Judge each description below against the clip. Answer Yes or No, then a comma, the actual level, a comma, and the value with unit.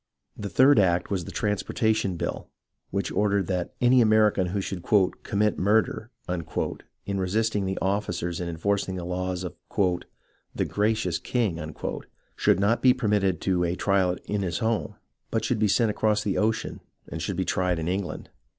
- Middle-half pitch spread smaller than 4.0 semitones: Yes, average, 3.0 semitones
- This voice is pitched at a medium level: No, low, 100 Hz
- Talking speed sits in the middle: Yes, average, 170 wpm